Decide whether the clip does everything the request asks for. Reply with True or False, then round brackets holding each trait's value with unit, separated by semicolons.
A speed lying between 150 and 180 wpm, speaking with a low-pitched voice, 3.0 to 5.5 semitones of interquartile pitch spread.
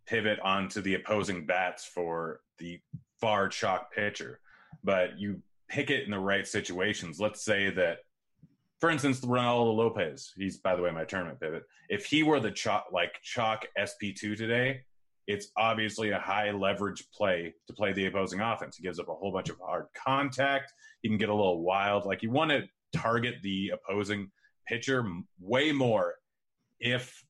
True (170 wpm; 105 Hz; 3.4 semitones)